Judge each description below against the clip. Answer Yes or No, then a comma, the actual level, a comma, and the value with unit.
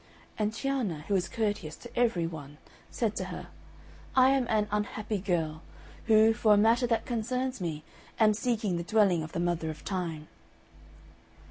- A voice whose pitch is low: No, high, 210 Hz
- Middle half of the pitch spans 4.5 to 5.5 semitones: Yes, average, 5.1 semitones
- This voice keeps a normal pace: Yes, average, 165 wpm